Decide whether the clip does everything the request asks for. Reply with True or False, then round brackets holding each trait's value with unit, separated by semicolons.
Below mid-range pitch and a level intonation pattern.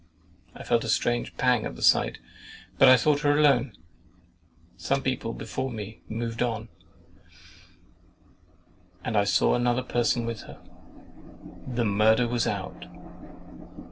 True (120 Hz; 2.2 semitones)